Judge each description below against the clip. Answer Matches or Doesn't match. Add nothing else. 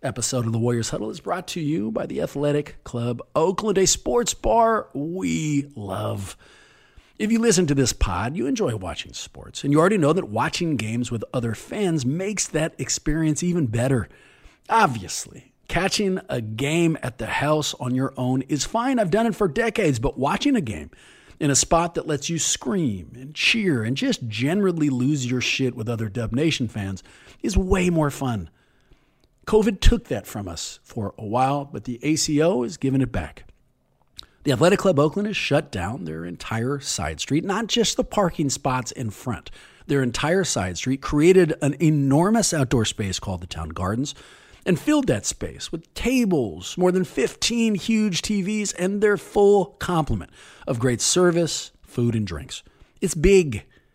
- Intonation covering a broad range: Matches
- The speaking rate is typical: Matches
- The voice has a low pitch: Doesn't match